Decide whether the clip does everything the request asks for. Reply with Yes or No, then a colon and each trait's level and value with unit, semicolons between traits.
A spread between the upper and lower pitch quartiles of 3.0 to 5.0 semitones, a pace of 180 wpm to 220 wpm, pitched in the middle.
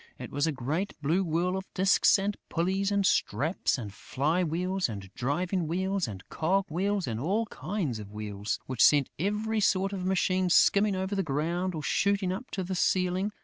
Yes: average, 4.7 semitones; average, 190 wpm; medium, 180 Hz